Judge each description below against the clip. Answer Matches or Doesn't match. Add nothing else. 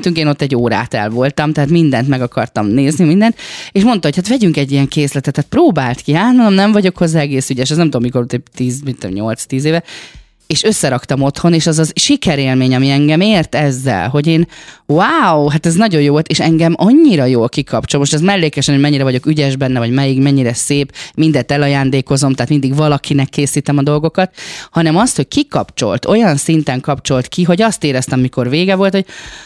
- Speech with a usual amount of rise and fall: Matches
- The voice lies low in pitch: Doesn't match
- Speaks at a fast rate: Matches